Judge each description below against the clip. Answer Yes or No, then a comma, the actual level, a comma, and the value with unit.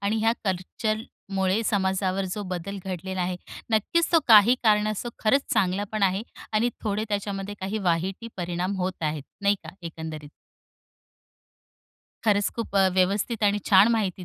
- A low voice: No, high, 200 Hz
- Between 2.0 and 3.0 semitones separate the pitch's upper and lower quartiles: Yes, narrow, 2.5 semitones